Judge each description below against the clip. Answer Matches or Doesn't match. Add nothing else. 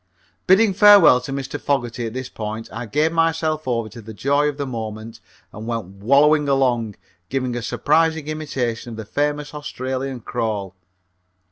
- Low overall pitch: Matches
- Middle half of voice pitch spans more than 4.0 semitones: Matches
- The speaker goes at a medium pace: Matches